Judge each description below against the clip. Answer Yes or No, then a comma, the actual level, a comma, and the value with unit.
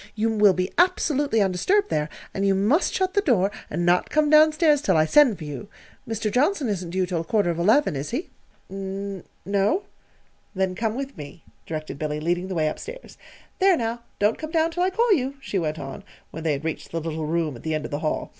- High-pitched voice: Yes, high, 200 Hz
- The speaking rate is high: Yes, fast, 230 wpm